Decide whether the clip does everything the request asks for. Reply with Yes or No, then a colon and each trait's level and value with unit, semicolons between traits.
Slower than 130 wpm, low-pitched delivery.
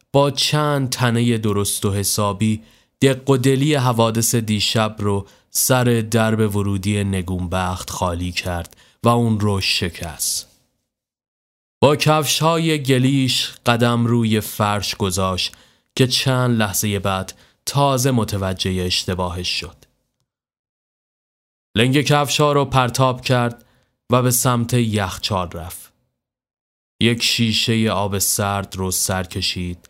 Yes: average, 110 wpm; low, 110 Hz